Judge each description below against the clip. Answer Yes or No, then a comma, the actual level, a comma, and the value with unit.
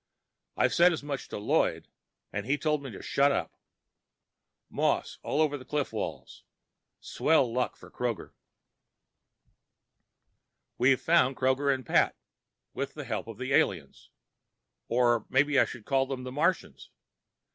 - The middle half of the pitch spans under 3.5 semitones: Yes, average, 2.8 semitones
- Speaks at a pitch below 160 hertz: Yes, low, 135 Hz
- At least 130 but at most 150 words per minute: Yes, average, 145 wpm